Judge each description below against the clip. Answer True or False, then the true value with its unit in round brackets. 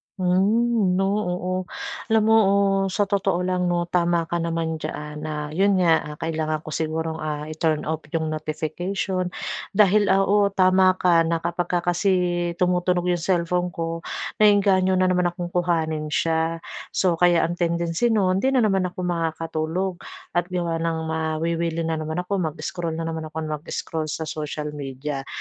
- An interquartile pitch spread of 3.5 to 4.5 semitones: False (2.5 semitones)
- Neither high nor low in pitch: True (170 Hz)